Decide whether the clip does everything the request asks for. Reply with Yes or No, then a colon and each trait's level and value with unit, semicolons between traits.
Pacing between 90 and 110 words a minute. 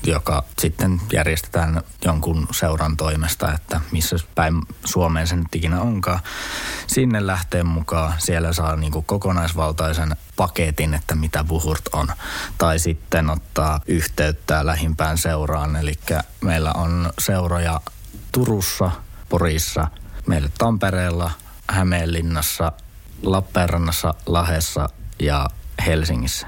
Yes: average, 100 wpm